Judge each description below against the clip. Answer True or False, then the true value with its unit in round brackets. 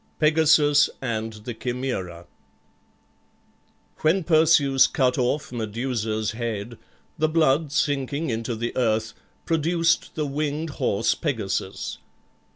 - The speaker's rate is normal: False (100 wpm)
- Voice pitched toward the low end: True (130 Hz)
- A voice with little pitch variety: False (5.3 semitones)